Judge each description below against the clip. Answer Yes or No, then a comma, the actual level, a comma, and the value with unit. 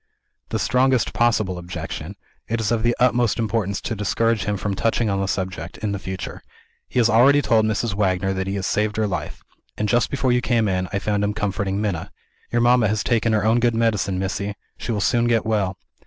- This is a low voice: Yes, low, 105 Hz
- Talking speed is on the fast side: Yes, fast, 215 wpm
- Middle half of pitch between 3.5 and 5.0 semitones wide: No, average, 3.0 semitones